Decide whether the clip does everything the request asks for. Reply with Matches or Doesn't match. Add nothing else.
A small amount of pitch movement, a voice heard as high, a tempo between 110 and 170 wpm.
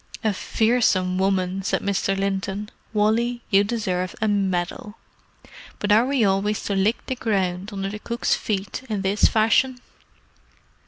Matches